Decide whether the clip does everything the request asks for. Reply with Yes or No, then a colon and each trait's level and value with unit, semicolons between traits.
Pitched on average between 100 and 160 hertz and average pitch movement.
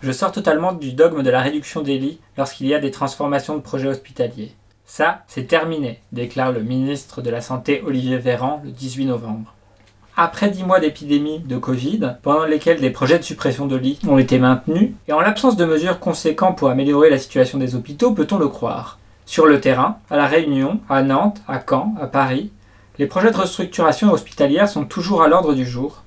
Yes: medium, 140 Hz; average, 4.0 semitones